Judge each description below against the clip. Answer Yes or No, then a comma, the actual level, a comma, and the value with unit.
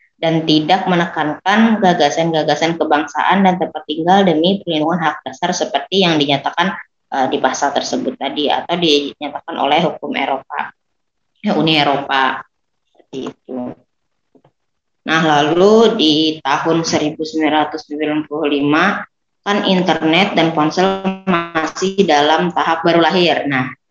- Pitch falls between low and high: Yes, medium, 160 Hz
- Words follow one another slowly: No, average, 110 wpm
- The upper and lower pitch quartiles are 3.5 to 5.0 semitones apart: No, average, 2.7 semitones